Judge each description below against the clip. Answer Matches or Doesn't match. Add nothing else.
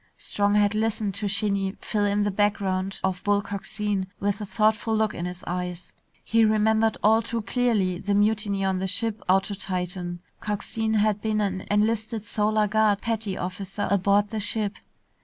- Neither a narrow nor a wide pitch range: Doesn't match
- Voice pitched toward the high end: Matches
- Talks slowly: Doesn't match